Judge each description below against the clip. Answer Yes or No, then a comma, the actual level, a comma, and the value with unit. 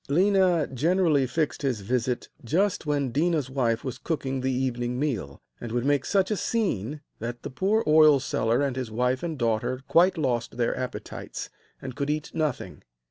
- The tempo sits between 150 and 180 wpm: Yes, average, 175 wpm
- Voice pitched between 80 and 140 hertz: Yes, low, 135 Hz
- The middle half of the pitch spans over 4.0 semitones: Yes, average, 4.4 semitones